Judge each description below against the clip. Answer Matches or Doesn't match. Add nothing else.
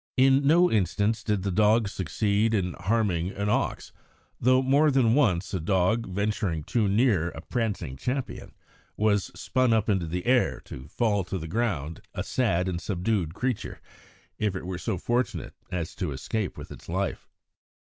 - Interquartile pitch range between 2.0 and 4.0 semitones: Doesn't match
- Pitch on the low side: Matches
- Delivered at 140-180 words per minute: Matches